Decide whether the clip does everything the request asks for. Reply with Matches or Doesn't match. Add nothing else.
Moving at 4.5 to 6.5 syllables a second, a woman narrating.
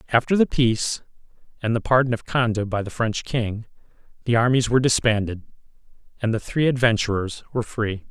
Doesn't match